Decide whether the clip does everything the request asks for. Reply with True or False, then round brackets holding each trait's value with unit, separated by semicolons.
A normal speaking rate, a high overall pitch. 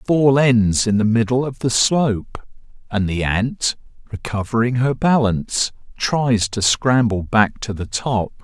False (155 wpm; 115 Hz)